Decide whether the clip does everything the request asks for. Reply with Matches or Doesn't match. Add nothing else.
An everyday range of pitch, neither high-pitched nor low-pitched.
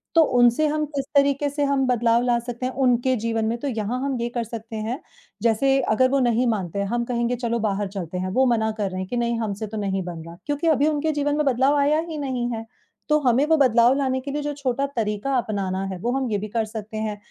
Doesn't match